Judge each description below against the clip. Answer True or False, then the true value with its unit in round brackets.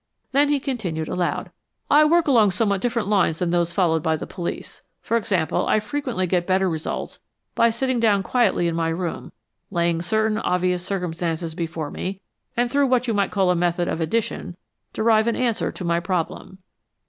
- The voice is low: False (190 Hz)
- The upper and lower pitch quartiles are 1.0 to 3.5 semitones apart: False (5.1 semitones)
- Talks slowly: False (185 wpm)